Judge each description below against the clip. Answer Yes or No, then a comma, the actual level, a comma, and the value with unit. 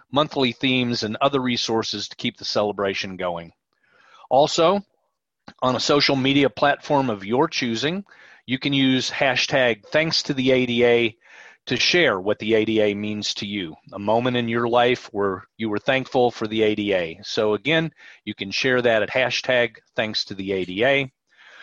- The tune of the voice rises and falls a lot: No, average, 4.3 semitones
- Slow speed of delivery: No, average, 165 wpm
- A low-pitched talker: Yes, low, 120 Hz